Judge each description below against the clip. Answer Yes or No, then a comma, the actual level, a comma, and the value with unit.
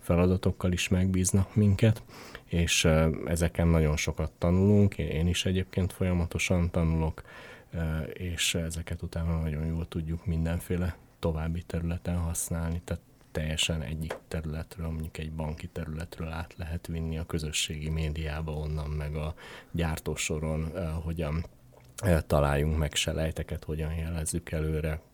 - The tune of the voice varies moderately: No, narrow, 2.0 semitones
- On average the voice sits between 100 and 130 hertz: No, very low, 85 Hz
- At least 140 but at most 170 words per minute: No, average, 115 wpm